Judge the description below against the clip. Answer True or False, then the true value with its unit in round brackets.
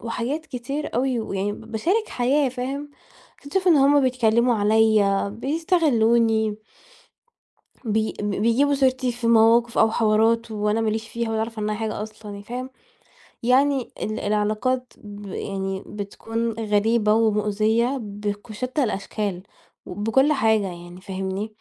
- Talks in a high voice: True (225 Hz)